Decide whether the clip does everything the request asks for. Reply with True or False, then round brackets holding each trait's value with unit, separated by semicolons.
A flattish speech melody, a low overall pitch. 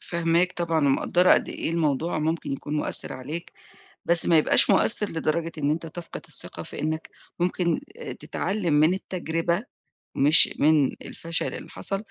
False (2.1 semitones; 165 Hz)